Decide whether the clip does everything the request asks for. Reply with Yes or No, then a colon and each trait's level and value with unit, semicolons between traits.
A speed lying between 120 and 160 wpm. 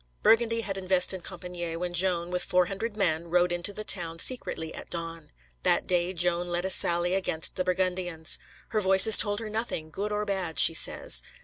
No: average, 190 wpm